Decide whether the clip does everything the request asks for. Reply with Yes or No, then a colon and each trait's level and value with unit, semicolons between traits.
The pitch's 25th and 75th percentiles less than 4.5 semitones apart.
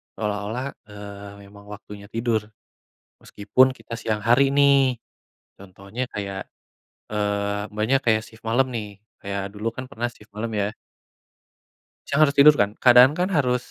Yes: average, 3.8 semitones